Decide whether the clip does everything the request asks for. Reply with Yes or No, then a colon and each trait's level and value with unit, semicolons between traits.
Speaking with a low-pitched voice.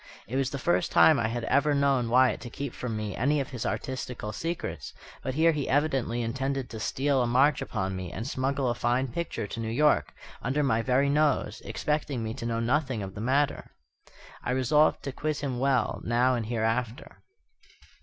Yes: low, 130 Hz